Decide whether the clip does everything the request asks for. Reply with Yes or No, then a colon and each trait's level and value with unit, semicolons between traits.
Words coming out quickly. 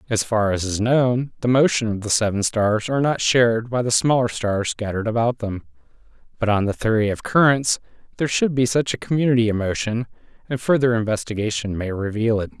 No: average, 195 wpm